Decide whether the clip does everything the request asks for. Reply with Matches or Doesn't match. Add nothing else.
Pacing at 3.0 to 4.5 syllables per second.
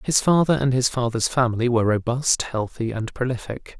Doesn't match